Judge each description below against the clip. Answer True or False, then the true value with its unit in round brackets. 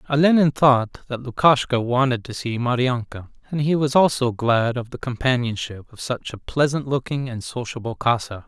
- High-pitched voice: False (125 Hz)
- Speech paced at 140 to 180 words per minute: True (170 wpm)